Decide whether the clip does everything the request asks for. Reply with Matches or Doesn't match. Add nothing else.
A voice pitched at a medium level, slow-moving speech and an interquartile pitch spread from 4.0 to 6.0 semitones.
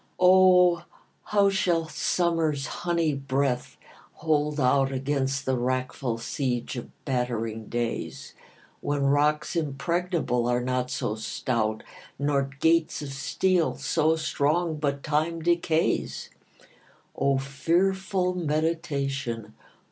Matches